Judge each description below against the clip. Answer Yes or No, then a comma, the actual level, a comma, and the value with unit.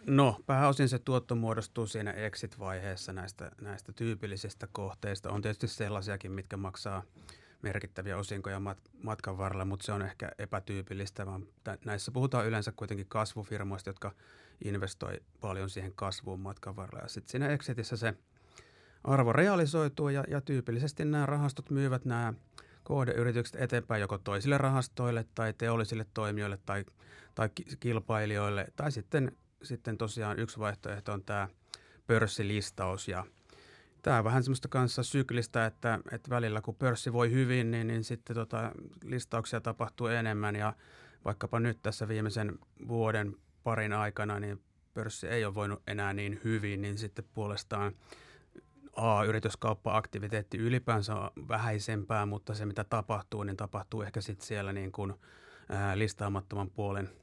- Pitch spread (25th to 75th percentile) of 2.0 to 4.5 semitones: Yes, average, 2.8 semitones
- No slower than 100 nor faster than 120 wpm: No, average, 135 wpm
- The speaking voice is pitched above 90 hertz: Yes, low, 110 Hz